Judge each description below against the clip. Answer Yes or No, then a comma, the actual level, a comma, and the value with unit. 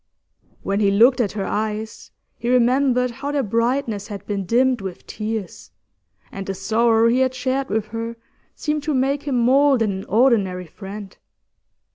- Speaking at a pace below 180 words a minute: Yes, average, 165 wpm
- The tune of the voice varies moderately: Yes, average, 4.0 semitones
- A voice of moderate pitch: No, high, 230 Hz